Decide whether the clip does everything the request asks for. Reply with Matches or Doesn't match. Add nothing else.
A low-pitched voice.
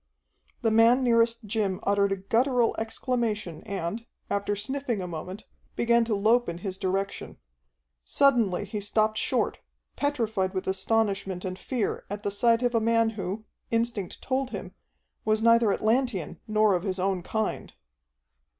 Doesn't match